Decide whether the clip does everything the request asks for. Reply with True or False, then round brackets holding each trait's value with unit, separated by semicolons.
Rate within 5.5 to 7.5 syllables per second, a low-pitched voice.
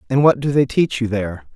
True (6.3 syllables/s; 125 Hz)